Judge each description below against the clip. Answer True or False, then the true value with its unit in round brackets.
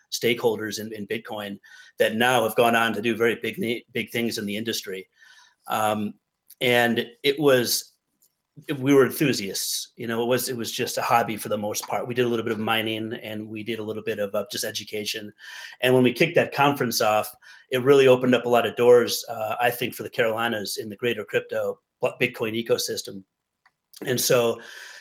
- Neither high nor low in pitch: False (115 Hz)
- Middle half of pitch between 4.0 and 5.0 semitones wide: False (2.8 semitones)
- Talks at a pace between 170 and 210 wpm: True (200 wpm)